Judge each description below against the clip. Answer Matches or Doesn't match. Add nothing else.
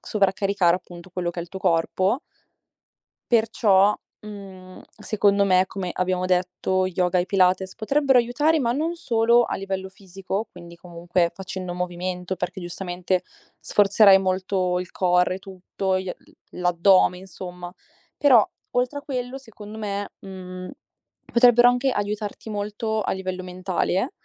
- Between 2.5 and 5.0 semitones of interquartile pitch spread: Matches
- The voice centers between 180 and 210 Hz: Matches